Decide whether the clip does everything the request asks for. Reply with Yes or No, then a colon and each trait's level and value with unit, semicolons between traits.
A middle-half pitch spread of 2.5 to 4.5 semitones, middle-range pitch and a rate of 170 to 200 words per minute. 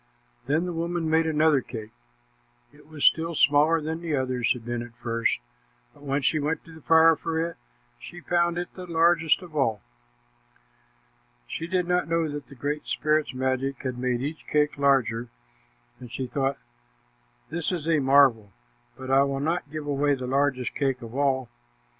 Yes: average, 3.7 semitones; medium, 145 Hz; average, 175 wpm